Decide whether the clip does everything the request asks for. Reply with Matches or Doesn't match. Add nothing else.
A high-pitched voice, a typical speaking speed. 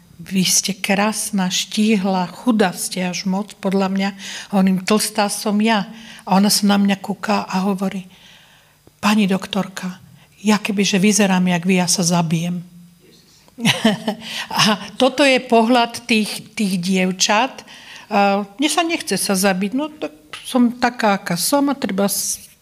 Matches